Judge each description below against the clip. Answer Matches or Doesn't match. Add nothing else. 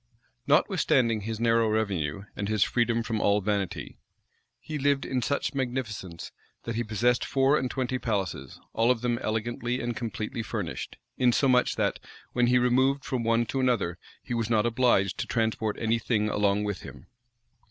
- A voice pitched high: Doesn't match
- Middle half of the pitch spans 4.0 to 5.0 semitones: Doesn't match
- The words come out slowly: Doesn't match